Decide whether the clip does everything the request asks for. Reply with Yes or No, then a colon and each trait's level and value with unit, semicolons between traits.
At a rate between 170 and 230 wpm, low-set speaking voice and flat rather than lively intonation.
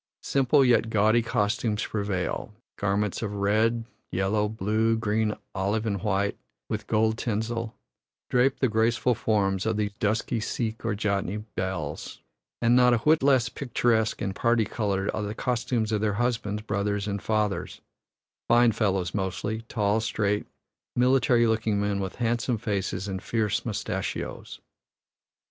No: average, 140 wpm; low, 110 Hz; narrow, 2.3 semitones